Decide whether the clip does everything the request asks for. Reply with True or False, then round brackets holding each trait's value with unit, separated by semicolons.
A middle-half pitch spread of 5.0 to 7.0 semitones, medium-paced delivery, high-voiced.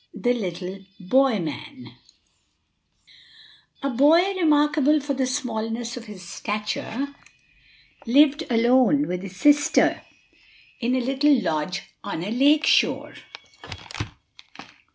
False (5.5 semitones; 105 wpm; 255 Hz)